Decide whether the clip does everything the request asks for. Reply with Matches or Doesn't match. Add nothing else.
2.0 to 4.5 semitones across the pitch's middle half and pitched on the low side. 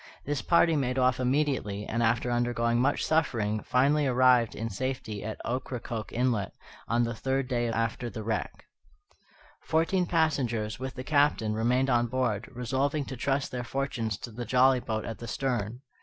Matches